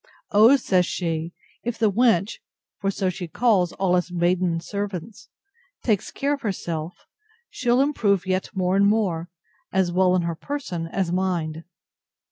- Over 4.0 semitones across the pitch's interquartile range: No, average, 3.4 semitones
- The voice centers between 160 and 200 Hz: Yes, medium, 185 Hz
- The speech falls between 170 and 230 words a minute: No, average, 150 wpm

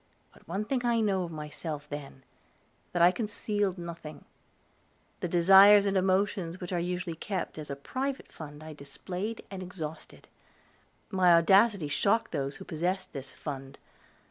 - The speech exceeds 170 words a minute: No, average, 150 wpm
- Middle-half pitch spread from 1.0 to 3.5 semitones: No, average, 4.3 semitones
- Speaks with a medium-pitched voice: Yes, medium, 180 Hz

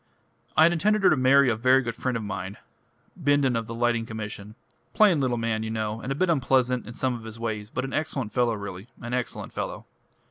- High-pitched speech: No, low, 120 Hz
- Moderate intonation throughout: Yes, average, 3.3 semitones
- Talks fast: Yes, fast, 225 wpm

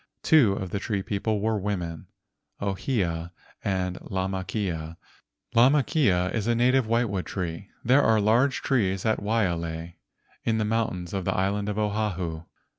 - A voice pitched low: Yes, low, 100 Hz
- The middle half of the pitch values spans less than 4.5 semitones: Yes, average, 3.6 semitones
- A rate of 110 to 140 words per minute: Yes, slow, 135 wpm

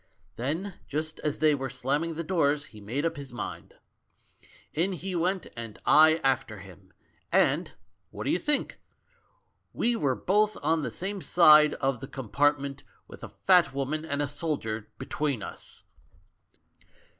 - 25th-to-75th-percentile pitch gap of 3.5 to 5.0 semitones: Yes, average, 3.9 semitones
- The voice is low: No, medium, 150 Hz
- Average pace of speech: Yes, average, 155 wpm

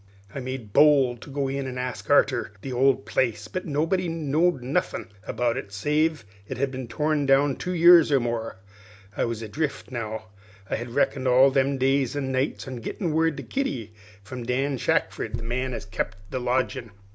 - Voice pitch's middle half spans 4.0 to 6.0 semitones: No, average, 3.2 semitones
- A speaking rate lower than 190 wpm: No, average, 195 wpm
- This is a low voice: Yes, low, 130 Hz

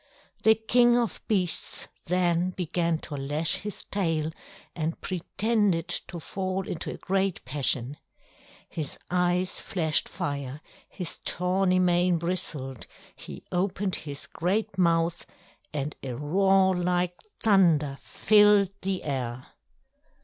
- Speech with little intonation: No, average, 3.7 semitones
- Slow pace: Yes, slow, 115 wpm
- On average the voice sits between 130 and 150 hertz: No, medium, 180 Hz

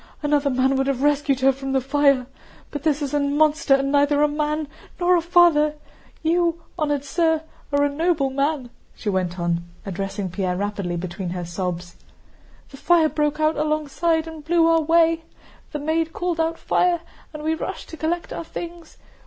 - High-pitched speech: Yes, very high, 295 Hz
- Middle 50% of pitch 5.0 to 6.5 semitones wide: No, average, 3.3 semitones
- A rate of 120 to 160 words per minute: No, average, 180 wpm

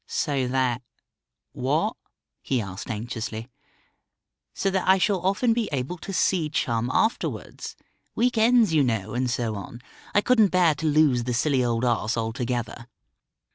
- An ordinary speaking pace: Yes, average, 150 wpm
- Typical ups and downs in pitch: No, wide, 7.7 semitones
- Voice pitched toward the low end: Yes, low, 130 Hz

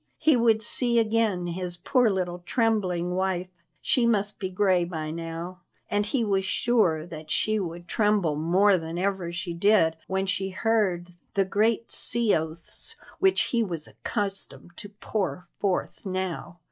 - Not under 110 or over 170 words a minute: Yes, average, 155 wpm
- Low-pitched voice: No, high, 190 Hz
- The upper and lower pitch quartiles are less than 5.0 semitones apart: Yes, average, 3.6 semitones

